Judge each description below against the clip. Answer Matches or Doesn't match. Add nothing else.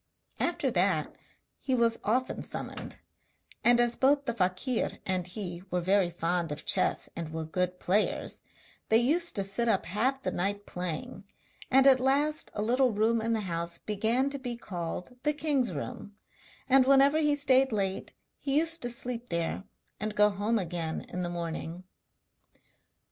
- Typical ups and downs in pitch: Doesn't match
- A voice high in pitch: Matches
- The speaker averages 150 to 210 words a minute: Matches